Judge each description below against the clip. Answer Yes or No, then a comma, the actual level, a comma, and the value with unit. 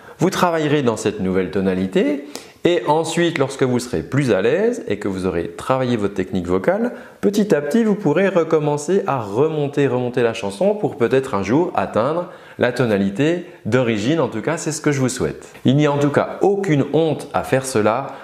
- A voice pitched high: No, medium, 140 Hz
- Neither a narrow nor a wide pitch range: No, wide, 7.2 semitones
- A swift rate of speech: No, average, 200 wpm